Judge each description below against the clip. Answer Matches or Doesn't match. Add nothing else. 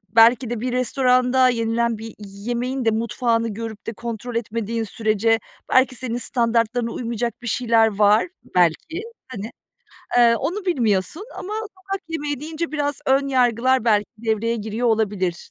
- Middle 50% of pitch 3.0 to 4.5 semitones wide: Doesn't match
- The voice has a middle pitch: Doesn't match